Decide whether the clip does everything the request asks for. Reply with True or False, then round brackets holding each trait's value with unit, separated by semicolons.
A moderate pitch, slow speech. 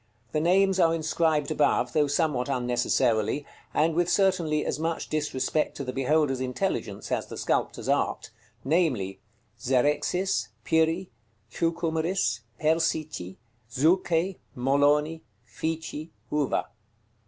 True (155 Hz; 110 wpm)